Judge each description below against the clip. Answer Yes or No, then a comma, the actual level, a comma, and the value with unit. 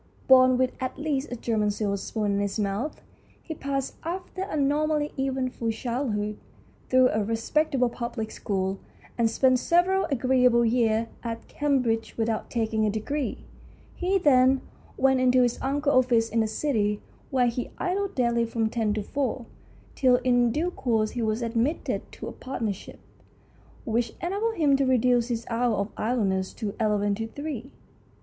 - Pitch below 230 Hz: No, high, 245 Hz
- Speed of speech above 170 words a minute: No, average, 160 wpm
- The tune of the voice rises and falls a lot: No, average, 3.6 semitones